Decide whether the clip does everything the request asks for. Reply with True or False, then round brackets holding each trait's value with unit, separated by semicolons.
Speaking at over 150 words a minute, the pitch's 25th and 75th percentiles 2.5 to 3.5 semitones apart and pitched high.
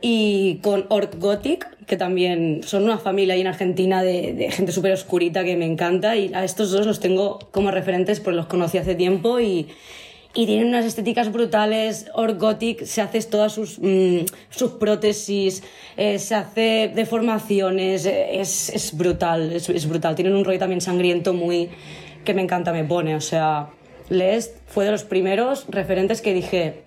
True (175 wpm; 2.9 semitones; 195 Hz)